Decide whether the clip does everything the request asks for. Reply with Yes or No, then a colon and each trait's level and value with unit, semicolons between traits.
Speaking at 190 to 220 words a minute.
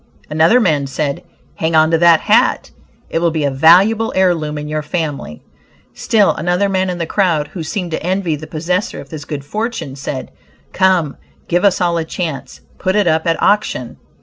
Yes: average, 195 wpm